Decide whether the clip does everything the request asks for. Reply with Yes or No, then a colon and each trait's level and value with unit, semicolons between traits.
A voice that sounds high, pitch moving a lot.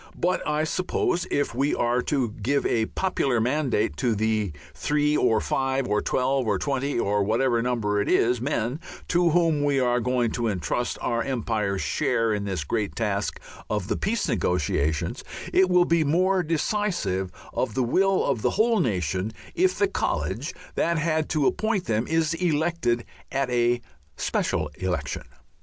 No: low, 125 Hz; wide, 6.6 semitones